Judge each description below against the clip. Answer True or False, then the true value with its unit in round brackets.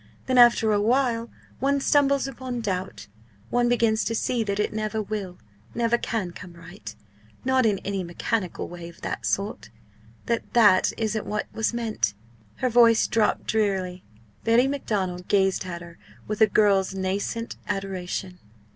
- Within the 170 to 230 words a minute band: False (155 wpm)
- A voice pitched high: True (215 Hz)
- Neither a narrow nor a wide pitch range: True (3.8 semitones)